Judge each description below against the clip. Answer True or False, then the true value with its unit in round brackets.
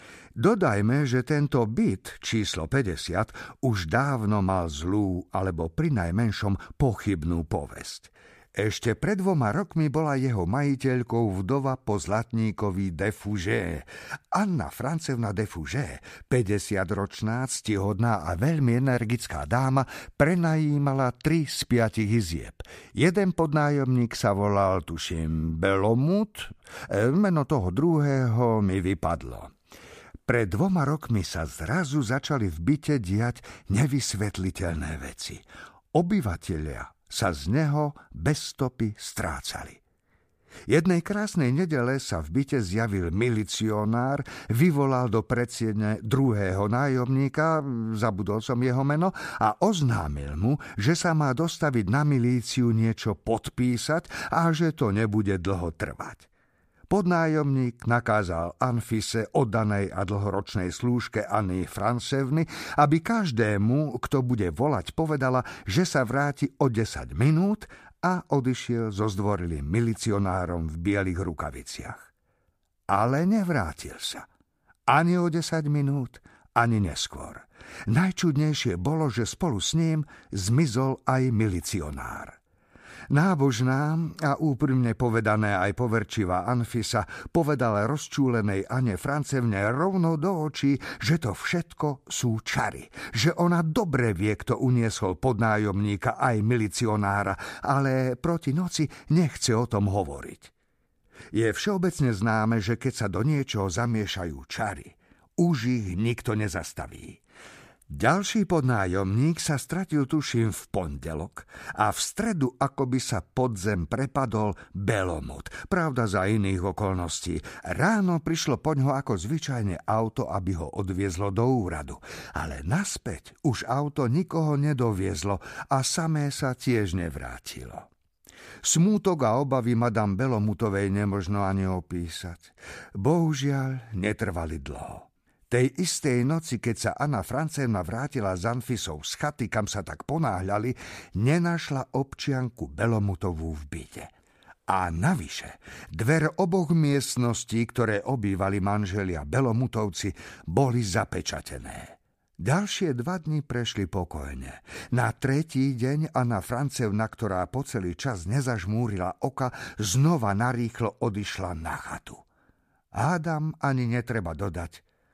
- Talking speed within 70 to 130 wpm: True (110 wpm)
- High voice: False (120 Hz)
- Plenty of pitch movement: True (6.0 semitones)